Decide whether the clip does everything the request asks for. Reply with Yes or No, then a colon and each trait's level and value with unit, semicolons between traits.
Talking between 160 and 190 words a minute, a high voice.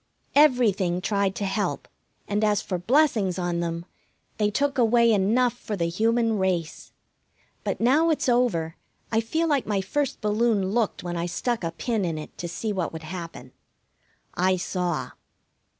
Yes: average, 165 wpm; high, 205 Hz